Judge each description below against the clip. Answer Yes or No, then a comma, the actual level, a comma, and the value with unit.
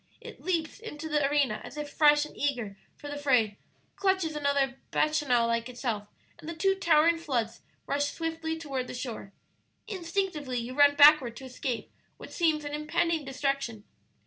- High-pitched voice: Yes, very high, 290 Hz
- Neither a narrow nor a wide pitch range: Yes, average, 4.0 semitones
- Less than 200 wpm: Yes, average, 165 wpm